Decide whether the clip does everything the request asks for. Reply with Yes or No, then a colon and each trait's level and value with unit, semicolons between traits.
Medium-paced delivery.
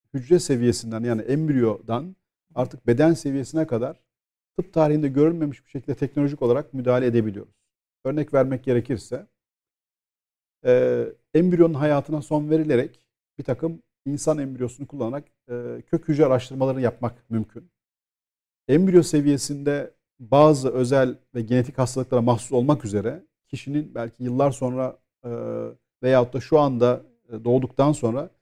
Yes: average, 120 wpm